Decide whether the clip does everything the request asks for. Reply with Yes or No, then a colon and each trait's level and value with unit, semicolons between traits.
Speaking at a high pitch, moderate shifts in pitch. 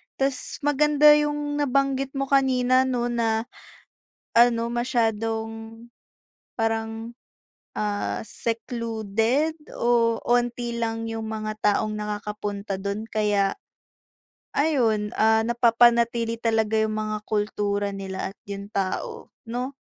No: high, 225 Hz; narrow, 2.3 semitones